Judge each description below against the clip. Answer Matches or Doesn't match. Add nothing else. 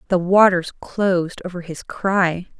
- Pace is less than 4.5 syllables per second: Matches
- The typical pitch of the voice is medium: Matches